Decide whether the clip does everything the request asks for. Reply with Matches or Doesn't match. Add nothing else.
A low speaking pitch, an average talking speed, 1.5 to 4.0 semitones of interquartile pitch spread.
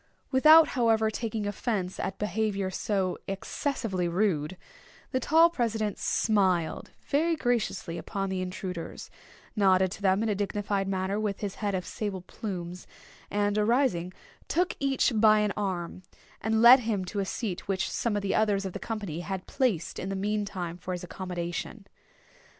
Doesn't match